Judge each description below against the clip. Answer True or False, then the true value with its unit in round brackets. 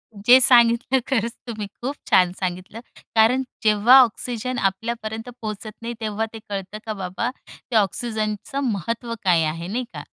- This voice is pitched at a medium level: False (220 Hz)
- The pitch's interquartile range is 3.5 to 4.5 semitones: False (3.0 semitones)